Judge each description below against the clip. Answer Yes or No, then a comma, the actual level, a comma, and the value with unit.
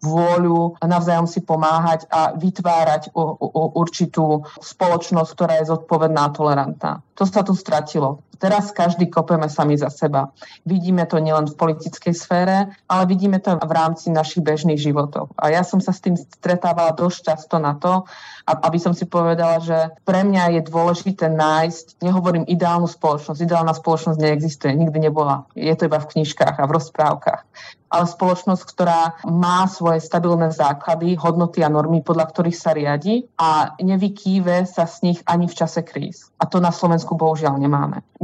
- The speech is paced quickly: Yes, fast, 170 wpm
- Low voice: No, medium, 165 Hz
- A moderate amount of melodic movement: No, narrow, 2.0 semitones